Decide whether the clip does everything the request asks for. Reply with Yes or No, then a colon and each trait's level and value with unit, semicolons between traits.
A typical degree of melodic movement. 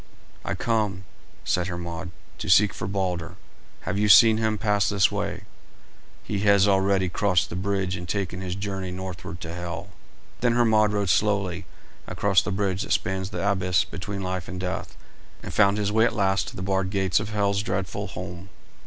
No: narrow, 2.0 semitones